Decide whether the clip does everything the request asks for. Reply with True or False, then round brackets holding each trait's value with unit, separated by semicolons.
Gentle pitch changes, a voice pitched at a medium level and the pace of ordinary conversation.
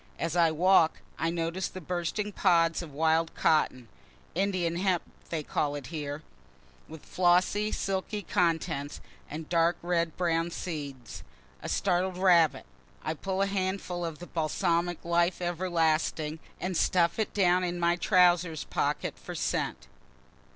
True (2.1 semitones; 170 Hz; 145 wpm)